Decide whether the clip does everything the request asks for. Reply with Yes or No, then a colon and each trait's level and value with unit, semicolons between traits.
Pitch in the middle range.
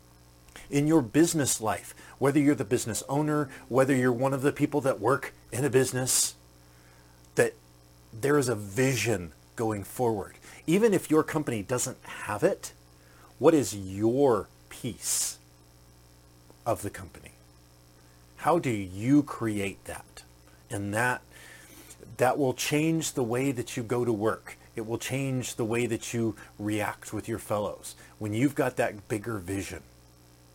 No: low, 110 Hz